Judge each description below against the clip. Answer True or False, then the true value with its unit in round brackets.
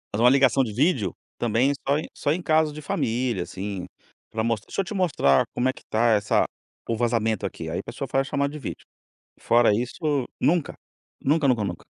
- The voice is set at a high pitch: False (125 Hz)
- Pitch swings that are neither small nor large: True (4.6 semitones)